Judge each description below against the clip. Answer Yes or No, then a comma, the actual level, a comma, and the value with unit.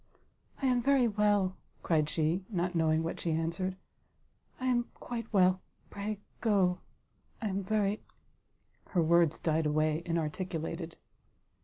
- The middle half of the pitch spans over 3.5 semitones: Yes, average, 4.3 semitones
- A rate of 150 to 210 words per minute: No, average, 140 wpm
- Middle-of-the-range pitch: Yes, medium, 180 Hz